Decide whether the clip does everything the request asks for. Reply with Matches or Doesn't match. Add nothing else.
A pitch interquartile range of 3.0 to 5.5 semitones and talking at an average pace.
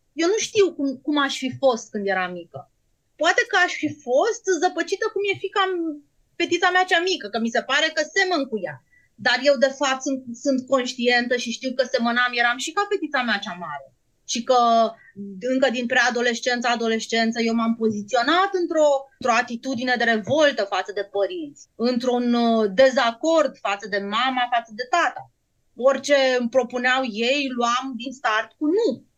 Doesn't match